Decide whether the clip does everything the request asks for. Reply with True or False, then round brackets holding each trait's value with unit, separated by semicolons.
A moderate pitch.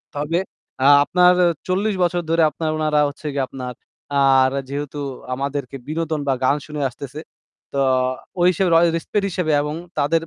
True (150 Hz)